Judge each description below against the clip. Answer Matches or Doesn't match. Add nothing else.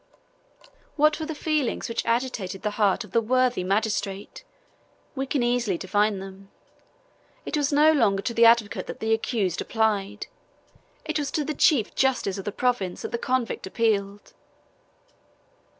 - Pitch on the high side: Matches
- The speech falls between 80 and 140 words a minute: Doesn't match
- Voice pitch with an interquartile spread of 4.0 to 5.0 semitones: Matches